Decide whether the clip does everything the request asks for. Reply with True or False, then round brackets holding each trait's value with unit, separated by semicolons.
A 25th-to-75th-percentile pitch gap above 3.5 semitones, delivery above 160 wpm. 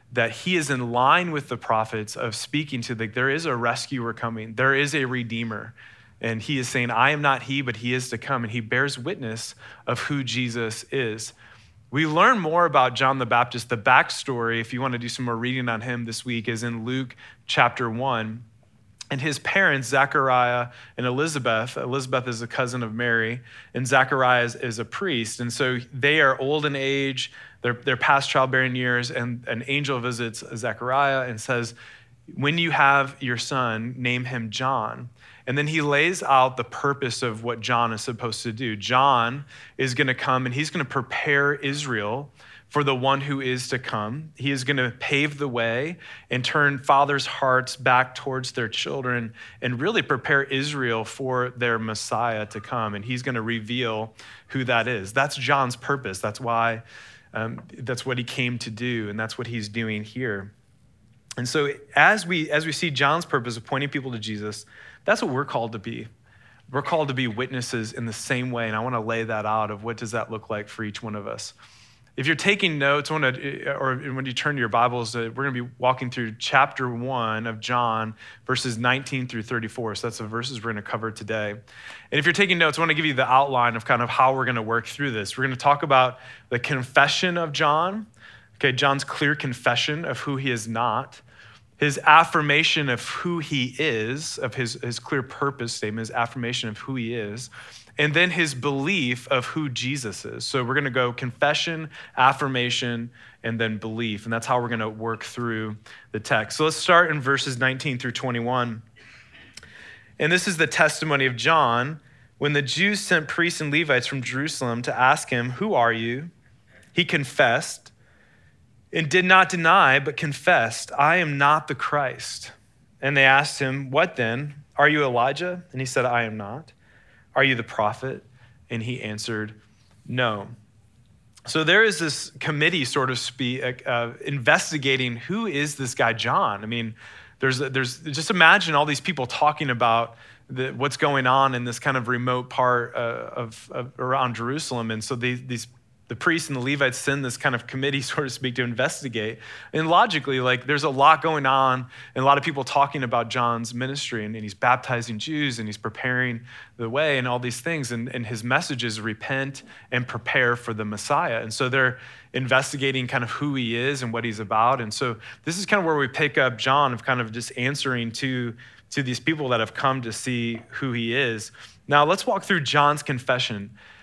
False (3.1 semitones; 195 wpm)